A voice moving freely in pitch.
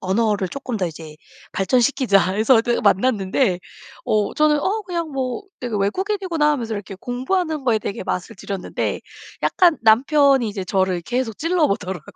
Yes: wide, 6.7 semitones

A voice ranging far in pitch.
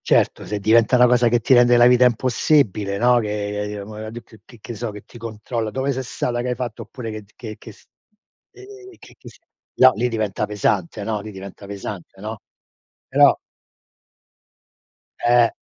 No: average, 2.8 semitones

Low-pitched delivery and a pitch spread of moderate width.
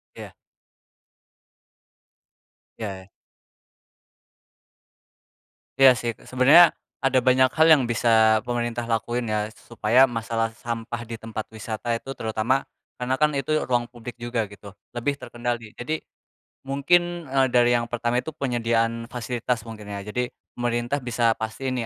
No: low, 120 Hz; narrow, 2.0 semitones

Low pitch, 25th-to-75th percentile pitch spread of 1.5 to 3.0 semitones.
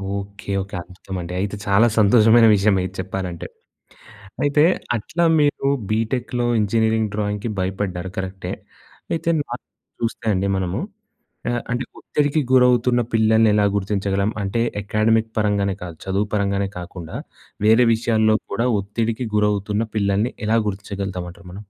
Yes: low, 105 Hz; average, 2.7 semitones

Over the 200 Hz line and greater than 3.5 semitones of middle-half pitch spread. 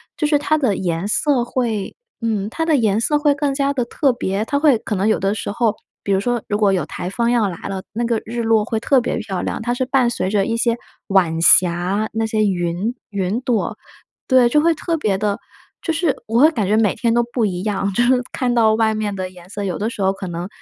Yes: high, 220 Hz; average, 3.9 semitones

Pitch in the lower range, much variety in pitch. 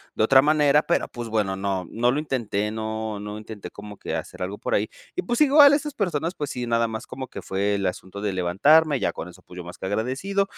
Yes: low, 110 Hz; wide, 6.7 semitones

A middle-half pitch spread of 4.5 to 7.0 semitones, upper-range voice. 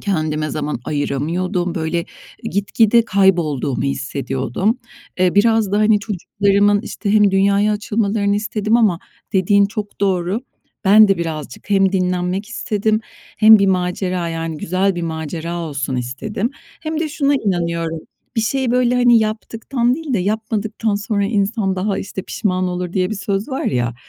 No: average, 4.0 semitones; high, 195 Hz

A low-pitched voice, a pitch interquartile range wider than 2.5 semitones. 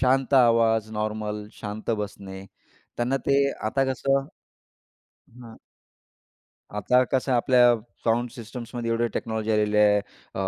Yes: low, 115 Hz; average, 2.9 semitones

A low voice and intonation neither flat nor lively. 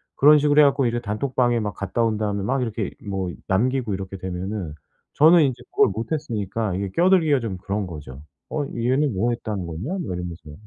No: low, 110 Hz; wide, 5.7 semitones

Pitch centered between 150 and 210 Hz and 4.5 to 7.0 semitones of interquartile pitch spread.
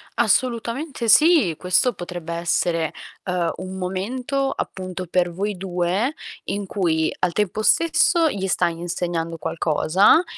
Yes: medium, 185 Hz; average, 5.1 semitones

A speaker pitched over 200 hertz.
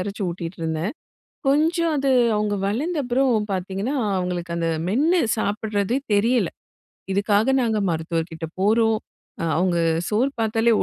Yes: high, 210 Hz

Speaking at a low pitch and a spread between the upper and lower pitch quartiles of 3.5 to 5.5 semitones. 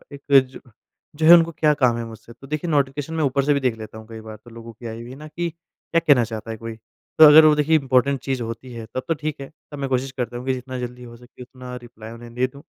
Yes: low, 130 Hz; average, 3.8 semitones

